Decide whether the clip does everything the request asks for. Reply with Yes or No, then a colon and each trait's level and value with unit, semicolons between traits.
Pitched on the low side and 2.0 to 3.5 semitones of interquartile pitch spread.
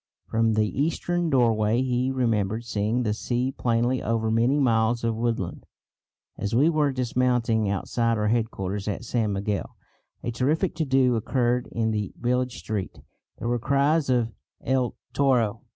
Yes: low, 120 Hz; narrow, 2.6 semitones